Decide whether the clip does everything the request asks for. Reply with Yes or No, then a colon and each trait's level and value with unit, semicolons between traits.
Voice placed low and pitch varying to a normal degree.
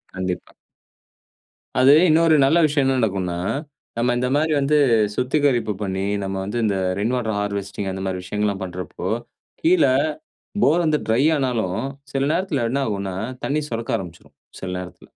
No: low, 115 Hz; wide, 6.4 semitones